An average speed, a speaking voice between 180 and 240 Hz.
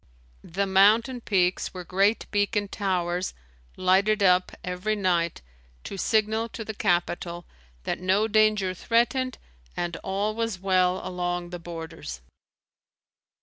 No: slow, 120 wpm; high, 190 Hz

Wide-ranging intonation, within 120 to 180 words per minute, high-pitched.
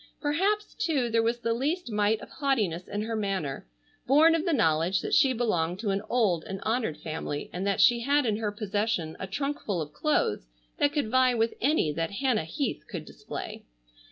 No: wide, 6.3 semitones; average, 200 wpm; high, 225 Hz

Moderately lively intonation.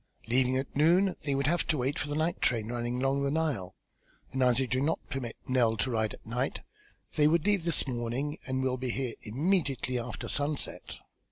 Yes: average, 3.3 semitones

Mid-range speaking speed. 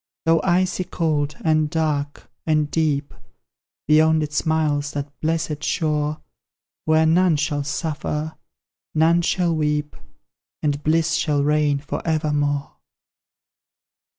No: slow, 110 wpm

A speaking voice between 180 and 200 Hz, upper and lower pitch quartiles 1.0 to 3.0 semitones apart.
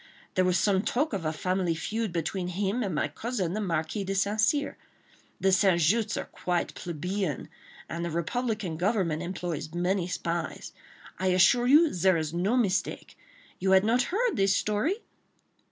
No: high, 190 Hz; average, 3.8 semitones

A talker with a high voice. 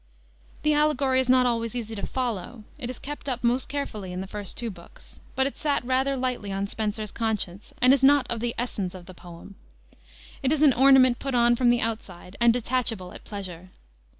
Yes: high, 240 Hz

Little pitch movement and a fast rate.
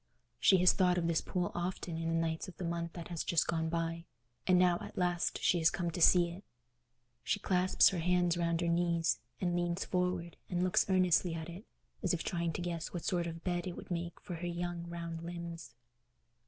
Yes: narrow, 1.2 semitones; fast, 220 wpm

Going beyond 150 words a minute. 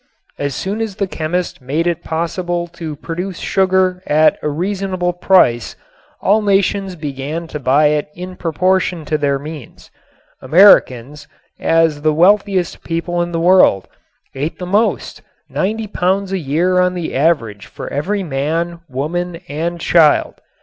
No: average, 145 wpm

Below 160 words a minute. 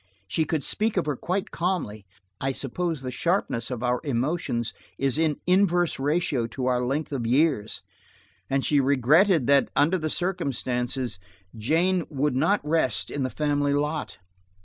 Yes: average, 150 wpm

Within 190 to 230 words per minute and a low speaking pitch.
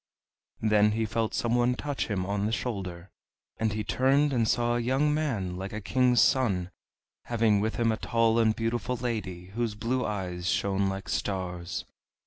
No: average, 175 wpm; low, 110 Hz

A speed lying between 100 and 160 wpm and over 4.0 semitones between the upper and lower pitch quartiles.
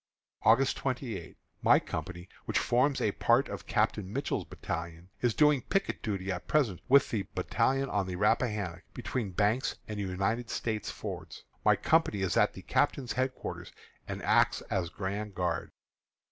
Yes: average, 155 wpm; average, 5.3 semitones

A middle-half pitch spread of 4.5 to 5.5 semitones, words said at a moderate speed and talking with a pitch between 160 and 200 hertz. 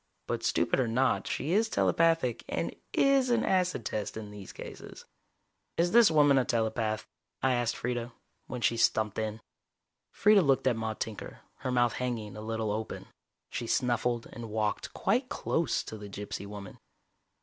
No: average, 4.9 semitones; average, 165 wpm; low, 120 Hz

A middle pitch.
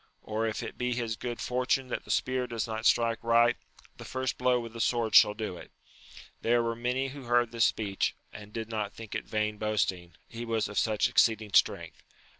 No: low, 115 Hz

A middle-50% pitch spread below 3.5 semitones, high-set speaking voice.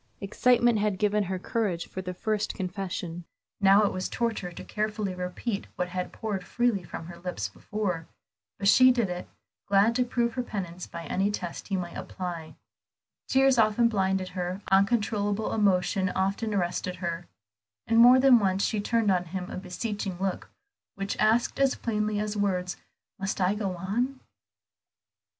Yes: average, 3.1 semitones; high, 195 Hz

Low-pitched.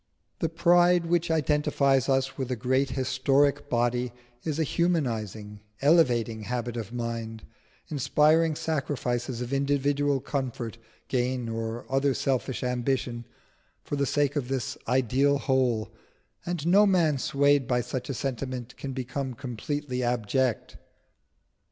Yes: low, 130 Hz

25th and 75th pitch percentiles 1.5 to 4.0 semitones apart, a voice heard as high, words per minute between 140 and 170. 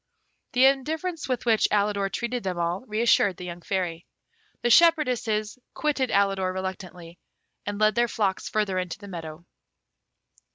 No: average, 4.6 semitones; high, 205 Hz; average, 150 wpm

